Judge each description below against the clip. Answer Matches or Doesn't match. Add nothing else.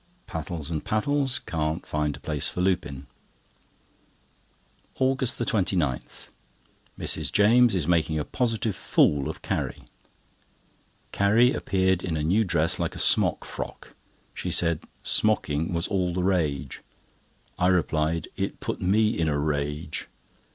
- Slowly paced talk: Matches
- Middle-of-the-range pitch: Doesn't match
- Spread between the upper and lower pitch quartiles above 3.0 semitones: Matches